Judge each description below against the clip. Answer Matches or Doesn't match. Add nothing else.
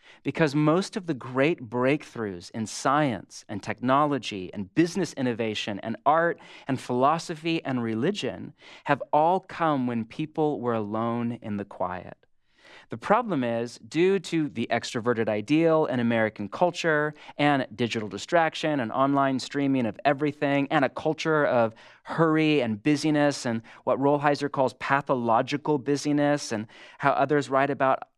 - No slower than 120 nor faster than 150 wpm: Matches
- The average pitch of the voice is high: Doesn't match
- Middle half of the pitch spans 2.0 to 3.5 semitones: Doesn't match